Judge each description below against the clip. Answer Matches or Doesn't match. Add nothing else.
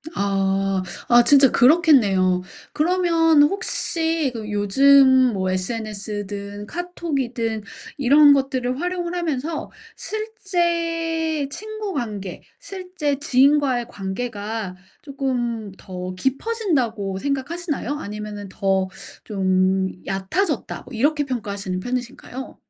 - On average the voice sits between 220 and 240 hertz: Doesn't match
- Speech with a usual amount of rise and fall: Doesn't match